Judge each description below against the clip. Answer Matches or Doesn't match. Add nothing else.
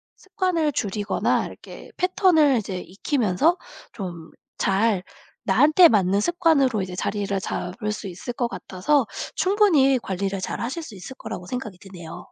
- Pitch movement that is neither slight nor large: Doesn't match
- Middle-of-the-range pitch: Doesn't match